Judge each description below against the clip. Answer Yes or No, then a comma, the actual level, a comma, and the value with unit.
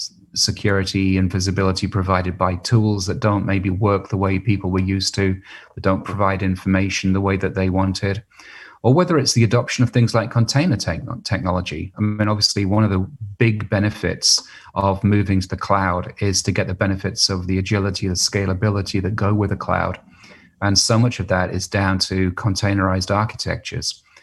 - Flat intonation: Yes, narrow, 1.8 semitones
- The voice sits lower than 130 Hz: Yes, low, 100 Hz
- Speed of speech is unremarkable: Yes, average, 185 wpm